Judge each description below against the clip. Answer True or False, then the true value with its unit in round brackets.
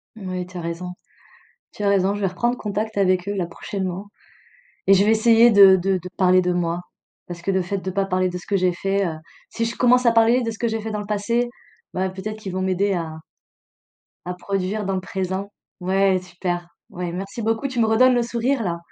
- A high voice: True (195 Hz)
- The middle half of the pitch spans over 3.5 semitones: False (3.2 semitones)